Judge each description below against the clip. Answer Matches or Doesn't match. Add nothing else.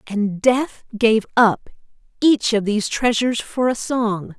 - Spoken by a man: Doesn't match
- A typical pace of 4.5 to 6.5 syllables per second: Doesn't match